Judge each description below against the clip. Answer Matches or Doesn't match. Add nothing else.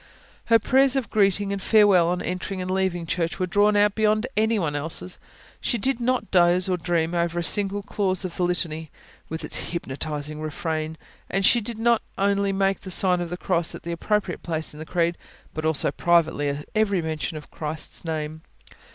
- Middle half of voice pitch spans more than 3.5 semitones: Matches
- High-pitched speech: Doesn't match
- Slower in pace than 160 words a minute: Doesn't match